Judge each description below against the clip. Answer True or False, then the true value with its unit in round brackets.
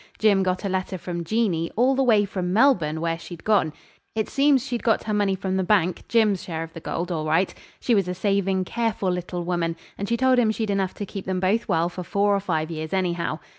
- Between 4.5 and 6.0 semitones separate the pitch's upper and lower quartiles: False (3.8 semitones)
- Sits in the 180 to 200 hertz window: True (190 Hz)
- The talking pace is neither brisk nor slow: False (240 wpm)